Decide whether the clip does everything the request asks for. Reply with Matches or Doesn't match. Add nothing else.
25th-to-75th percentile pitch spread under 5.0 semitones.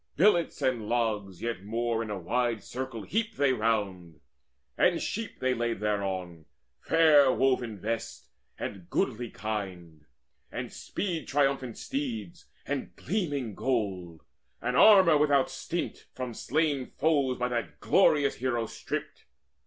Doesn't match